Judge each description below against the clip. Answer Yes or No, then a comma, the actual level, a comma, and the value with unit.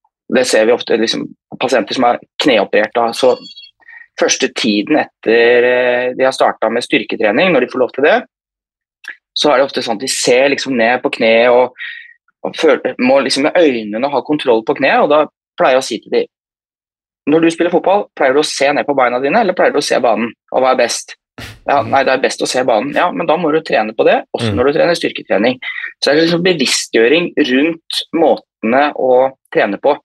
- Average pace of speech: No, fast, 215 wpm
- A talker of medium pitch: Yes, medium, 150 Hz